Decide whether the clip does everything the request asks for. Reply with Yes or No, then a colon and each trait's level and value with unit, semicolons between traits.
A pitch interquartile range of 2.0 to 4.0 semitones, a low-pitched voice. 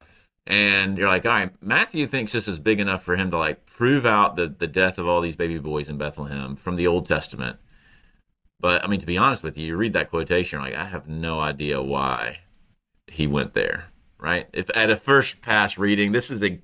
No: average, 4.7 semitones; very low, 90 Hz